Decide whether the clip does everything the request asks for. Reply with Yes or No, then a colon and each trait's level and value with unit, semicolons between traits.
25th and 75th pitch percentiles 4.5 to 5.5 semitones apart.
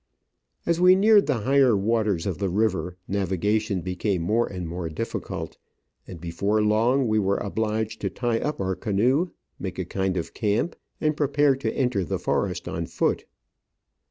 Yes: average, 5.1 semitones